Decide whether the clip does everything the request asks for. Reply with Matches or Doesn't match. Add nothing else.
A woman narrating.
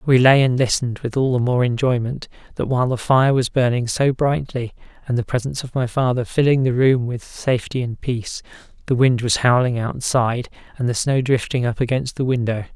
Doesn't match